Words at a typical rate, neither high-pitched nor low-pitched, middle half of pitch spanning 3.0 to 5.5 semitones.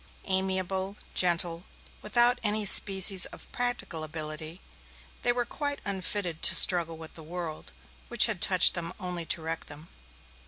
Yes: average, 145 wpm; medium, 180 Hz; average, 3.7 semitones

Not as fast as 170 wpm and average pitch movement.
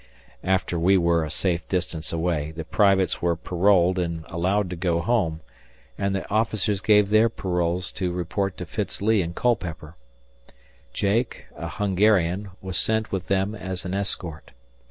Yes: average, 155 wpm; average, 3.0 semitones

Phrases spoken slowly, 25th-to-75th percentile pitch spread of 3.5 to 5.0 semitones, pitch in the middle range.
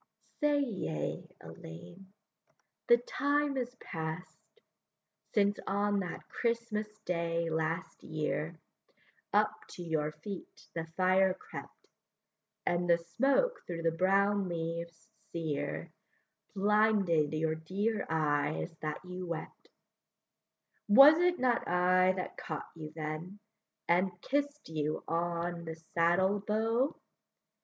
Yes: slow, 110 wpm; average, 4.4 semitones; medium, 180 Hz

